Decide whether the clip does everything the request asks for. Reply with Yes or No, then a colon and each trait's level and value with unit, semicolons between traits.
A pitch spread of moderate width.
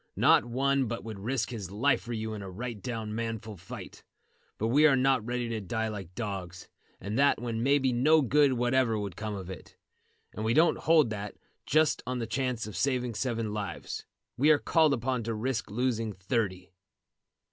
Yes: average, 3.6 semitones